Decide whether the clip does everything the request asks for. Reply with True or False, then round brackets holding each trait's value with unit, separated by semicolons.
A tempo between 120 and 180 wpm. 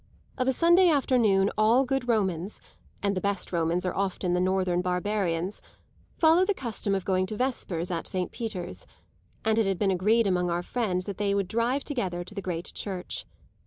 False (190 wpm)